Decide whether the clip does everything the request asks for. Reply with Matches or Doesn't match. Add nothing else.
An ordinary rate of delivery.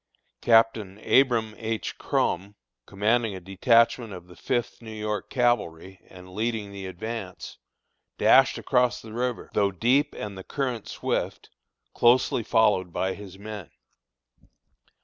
Doesn't match